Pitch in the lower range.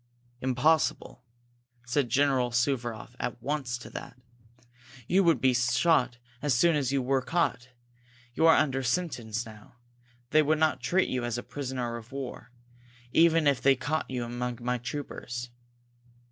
Yes: low, 130 Hz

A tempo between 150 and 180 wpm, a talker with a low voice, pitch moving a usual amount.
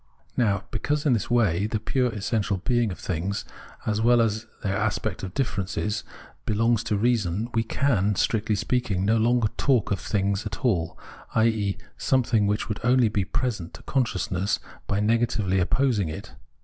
Yes: average, 165 wpm; low, 110 Hz; average, 3.0 semitones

